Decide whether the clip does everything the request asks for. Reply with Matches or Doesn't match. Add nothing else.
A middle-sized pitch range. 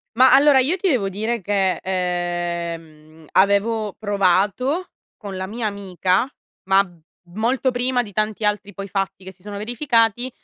Matches